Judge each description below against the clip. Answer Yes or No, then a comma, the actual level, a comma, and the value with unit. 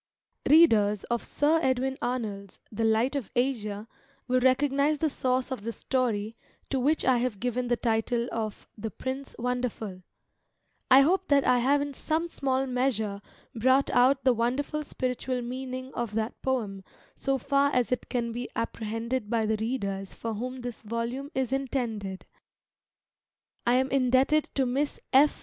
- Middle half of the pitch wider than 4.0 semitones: No, average, 2.9 semitones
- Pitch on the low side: No, very high, 250 Hz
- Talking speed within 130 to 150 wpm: No, average, 165 wpm